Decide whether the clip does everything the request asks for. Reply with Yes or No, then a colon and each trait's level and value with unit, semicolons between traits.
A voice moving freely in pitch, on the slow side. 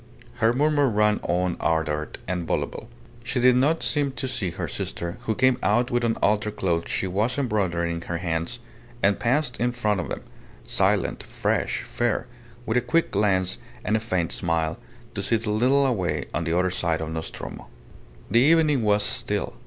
No: wide, 5.9 semitones; average, 185 wpm